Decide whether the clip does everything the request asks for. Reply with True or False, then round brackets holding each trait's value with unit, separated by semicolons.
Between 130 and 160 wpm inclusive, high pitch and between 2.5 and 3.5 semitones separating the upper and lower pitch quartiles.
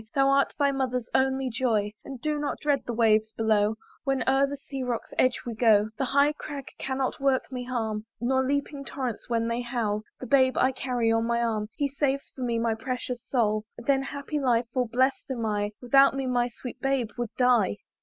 False (205 wpm; 250 Hz; 2.9 semitones)